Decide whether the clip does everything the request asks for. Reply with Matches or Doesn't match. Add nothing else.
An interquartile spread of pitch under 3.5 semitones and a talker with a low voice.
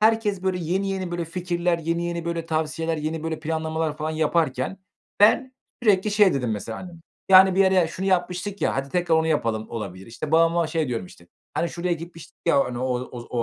Doesn't match